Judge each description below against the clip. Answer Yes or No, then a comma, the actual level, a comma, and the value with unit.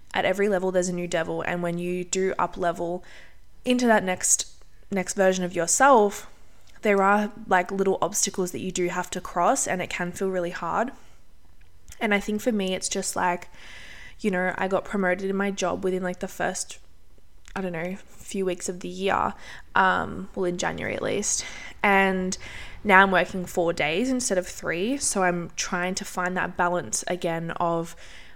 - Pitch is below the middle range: No, medium, 185 Hz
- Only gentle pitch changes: Yes, narrow, 1.8 semitones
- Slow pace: No, average, 190 wpm